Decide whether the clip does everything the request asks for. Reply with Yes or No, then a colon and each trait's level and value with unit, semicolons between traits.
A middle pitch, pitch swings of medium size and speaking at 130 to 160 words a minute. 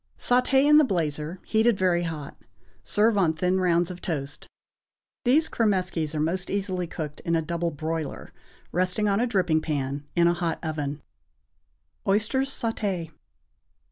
Yes: medium, 175 Hz; average, 4.6 semitones; average, 145 wpm